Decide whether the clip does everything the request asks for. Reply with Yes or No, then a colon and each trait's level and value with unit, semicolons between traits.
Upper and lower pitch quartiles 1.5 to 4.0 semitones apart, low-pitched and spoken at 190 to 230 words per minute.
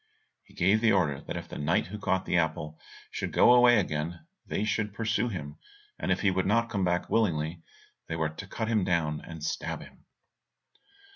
No: average, 5.1 semitones; very low, 90 Hz; average, 200 wpm